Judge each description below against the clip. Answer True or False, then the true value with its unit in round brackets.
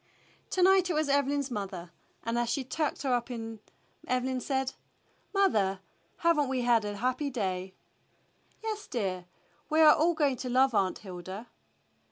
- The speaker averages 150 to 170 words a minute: True (160 wpm)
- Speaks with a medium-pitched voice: False (255 Hz)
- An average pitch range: False (6.1 semitones)